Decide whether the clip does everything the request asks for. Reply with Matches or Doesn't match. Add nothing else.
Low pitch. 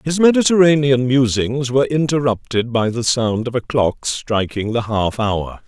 Matches